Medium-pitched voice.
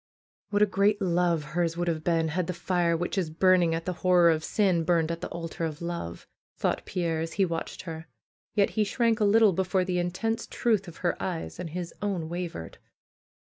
Yes: medium, 175 Hz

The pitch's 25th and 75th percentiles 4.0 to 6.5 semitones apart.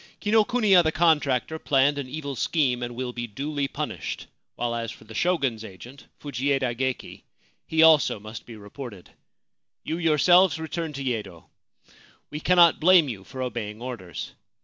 Yes: average, 5.1 semitones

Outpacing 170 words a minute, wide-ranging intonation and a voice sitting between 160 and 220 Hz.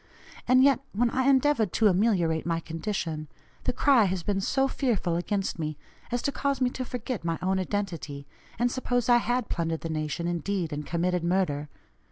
Yes: average, 185 wpm; wide, 6.7 semitones; high, 190 Hz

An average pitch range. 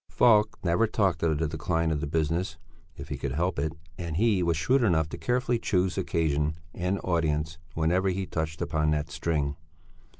Yes: average, 3.3 semitones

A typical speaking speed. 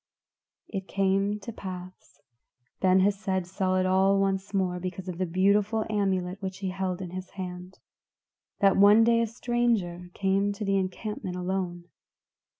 Yes: average, 150 wpm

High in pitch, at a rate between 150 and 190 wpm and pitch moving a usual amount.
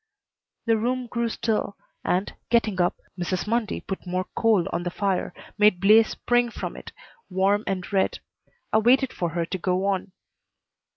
Yes: high, 200 Hz; average, 165 wpm; average, 3.6 semitones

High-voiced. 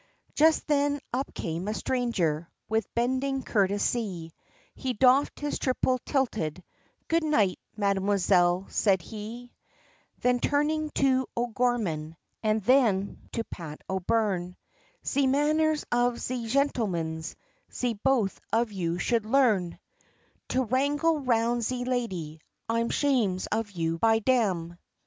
Yes: high, 230 Hz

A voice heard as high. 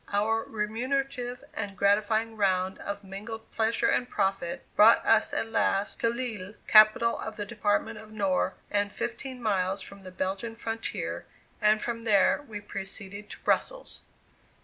Yes: high, 215 Hz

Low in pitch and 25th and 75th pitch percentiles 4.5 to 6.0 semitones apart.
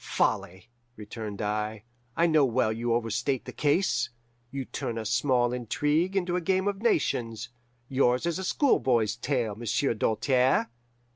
Yes: low, 125 Hz; average, 4.8 semitones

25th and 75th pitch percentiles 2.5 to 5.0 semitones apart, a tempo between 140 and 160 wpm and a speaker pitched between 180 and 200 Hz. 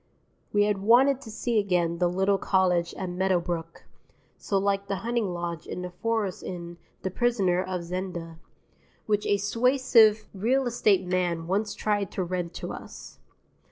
Yes: average, 3.2 semitones; average, 155 wpm; high, 190 Hz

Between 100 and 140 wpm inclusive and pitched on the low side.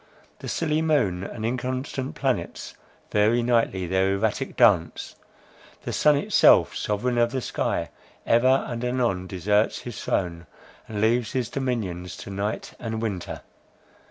Yes: slow, 135 wpm; low, 115 Hz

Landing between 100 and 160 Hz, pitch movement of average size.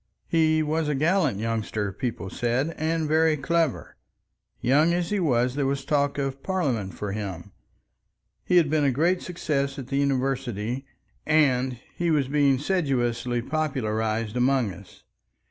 Yes: low, 135 Hz; average, 4.5 semitones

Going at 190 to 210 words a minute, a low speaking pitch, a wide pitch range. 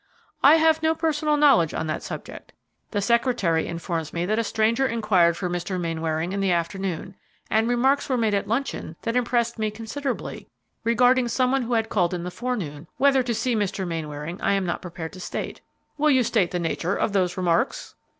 No: average, 200 wpm; high, 210 Hz; wide, 6.1 semitones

